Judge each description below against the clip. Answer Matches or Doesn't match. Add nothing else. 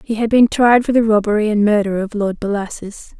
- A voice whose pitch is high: Matches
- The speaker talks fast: Matches